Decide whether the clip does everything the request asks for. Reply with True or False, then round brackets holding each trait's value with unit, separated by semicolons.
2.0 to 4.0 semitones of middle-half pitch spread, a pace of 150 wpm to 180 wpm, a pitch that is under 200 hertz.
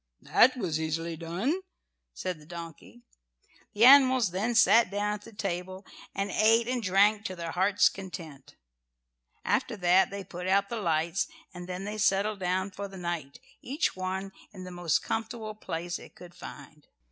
True (3.4 semitones; 170 wpm; 190 Hz)